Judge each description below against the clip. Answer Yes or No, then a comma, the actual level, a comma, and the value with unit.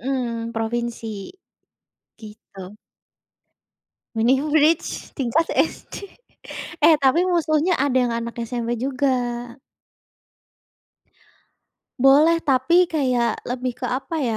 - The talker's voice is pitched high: Yes, very high, 255 Hz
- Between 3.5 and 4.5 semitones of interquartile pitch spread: Yes, average, 4.2 semitones